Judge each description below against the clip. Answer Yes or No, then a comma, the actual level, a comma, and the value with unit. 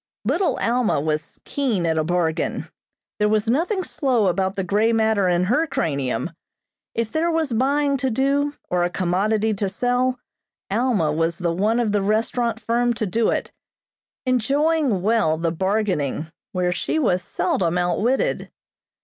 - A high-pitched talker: Yes, high, 215 Hz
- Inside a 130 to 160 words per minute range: Yes, average, 155 wpm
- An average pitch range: No, wide, 5.9 semitones